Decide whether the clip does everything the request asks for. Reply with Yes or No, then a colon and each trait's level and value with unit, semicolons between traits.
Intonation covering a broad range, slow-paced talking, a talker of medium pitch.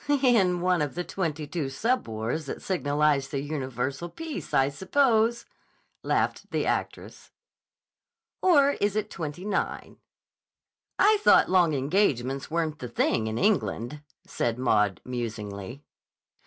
Yes: wide, 7.5 semitones; slow, 130 wpm; medium, 150 Hz